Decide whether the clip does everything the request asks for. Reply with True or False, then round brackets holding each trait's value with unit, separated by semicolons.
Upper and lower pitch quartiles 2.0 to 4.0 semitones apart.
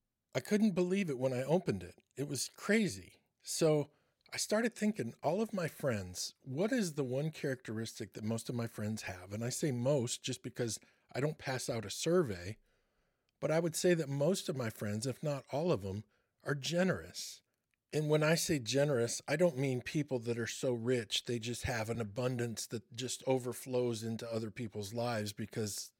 False (5.0 semitones)